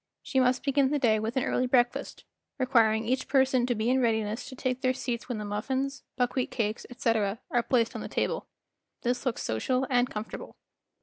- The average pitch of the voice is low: No, high, 245 Hz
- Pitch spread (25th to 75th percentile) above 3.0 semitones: No, narrow, 2.6 semitones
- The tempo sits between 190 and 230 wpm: Yes, average, 200 wpm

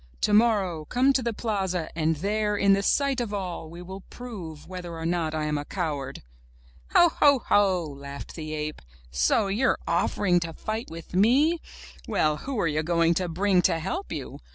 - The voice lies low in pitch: No, medium, 185 Hz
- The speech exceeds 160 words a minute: Yes, average, 185 wpm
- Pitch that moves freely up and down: No, average, 5.0 semitones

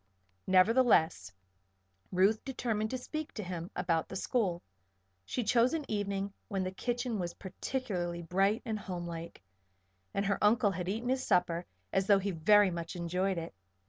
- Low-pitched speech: No, high, 195 Hz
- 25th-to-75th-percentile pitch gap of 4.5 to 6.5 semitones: No, average, 4.1 semitones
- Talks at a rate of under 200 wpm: Yes, average, 155 wpm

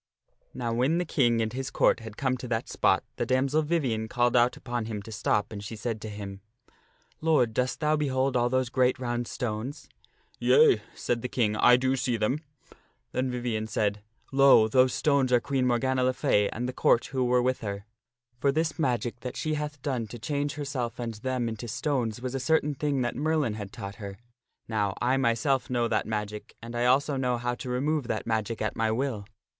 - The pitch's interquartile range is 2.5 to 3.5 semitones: Yes, average, 3.1 semitones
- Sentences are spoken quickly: Yes, fast, 215 wpm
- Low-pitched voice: Yes, low, 125 Hz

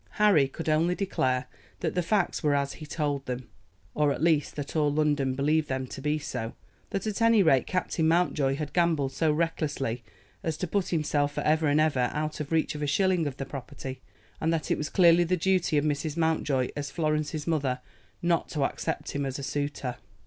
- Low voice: No, medium, 150 Hz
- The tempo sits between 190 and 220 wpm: Yes, fast, 205 wpm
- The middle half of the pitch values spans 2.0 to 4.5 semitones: Yes, average, 2.8 semitones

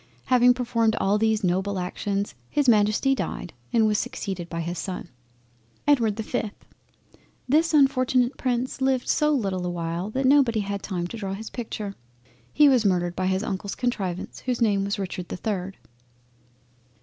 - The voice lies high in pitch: Yes, high, 210 Hz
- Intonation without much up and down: No, average, 4.7 semitones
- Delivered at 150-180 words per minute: Yes, average, 165 wpm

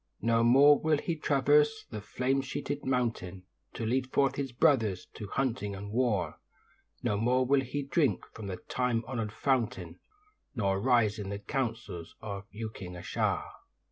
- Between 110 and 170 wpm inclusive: Yes, average, 160 wpm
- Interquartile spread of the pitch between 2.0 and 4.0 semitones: No, average, 4.7 semitones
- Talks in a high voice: No, low, 120 Hz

